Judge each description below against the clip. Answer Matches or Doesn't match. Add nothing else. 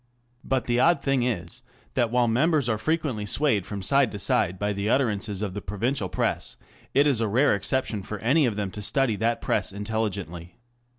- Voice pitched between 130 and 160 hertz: Doesn't match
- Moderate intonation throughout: Matches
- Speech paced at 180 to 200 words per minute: Matches